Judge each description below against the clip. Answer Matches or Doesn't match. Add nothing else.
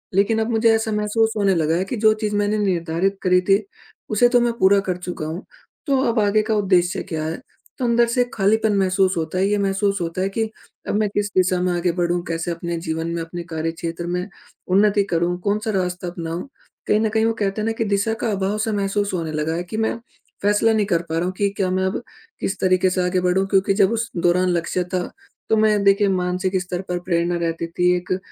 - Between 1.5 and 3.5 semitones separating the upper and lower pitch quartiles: Matches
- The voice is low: Doesn't match